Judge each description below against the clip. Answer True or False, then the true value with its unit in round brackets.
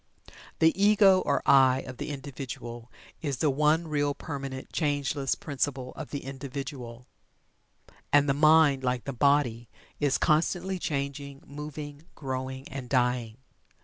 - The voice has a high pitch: False (140 Hz)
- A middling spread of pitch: False (2.3 semitones)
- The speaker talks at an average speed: False (130 wpm)